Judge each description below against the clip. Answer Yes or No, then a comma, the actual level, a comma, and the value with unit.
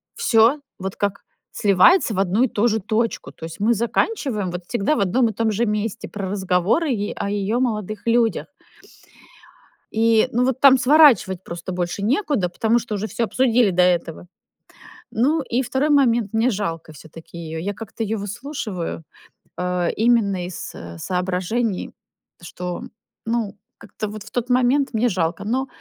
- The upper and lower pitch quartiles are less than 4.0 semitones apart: No, average, 4.5 semitones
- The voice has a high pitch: Yes, high, 215 Hz